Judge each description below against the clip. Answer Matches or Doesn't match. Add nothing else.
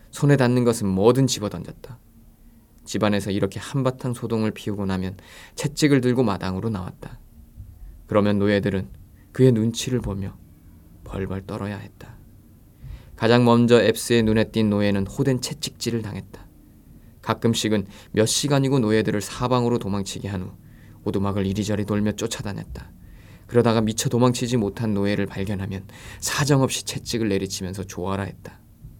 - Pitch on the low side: Matches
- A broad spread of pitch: Doesn't match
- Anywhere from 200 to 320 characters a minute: Doesn't match